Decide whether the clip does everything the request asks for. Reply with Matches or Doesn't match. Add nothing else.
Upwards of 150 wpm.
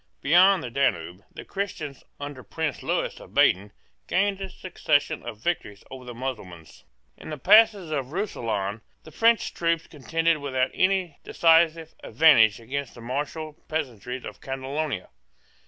Doesn't match